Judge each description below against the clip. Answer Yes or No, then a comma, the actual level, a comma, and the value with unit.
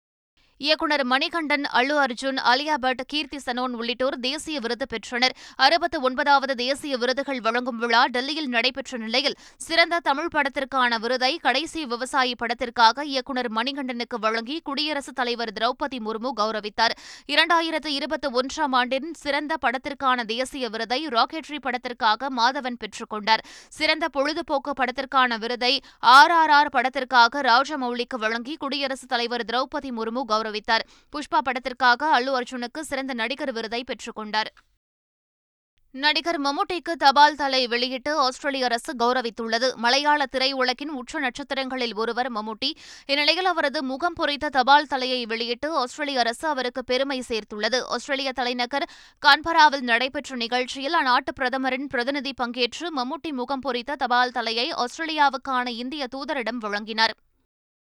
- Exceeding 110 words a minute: Yes, average, 120 wpm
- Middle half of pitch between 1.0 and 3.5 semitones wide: Yes, average, 3.2 semitones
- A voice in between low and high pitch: No, very high, 260 Hz